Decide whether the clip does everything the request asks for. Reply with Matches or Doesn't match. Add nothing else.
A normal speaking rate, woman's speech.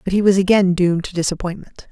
Doesn't match